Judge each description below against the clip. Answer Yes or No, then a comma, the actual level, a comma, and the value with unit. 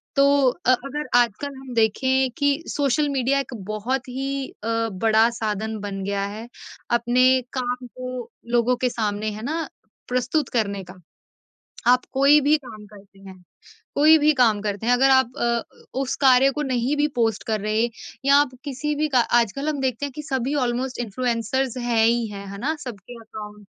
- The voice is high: Yes, high, 245 Hz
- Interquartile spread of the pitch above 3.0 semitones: Yes, average, 3.5 semitones